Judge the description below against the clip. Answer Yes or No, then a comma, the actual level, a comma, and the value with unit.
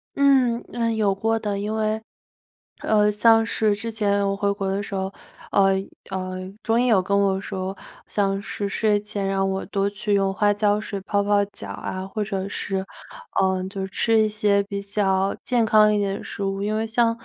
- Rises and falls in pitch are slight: Yes, narrow, 1.8 semitones